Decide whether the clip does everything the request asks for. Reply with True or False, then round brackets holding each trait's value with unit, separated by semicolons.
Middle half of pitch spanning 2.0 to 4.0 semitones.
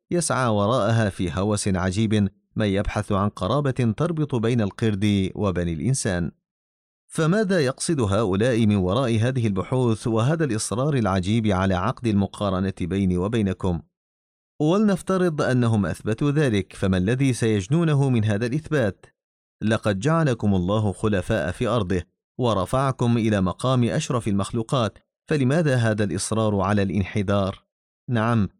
False (4.7 semitones)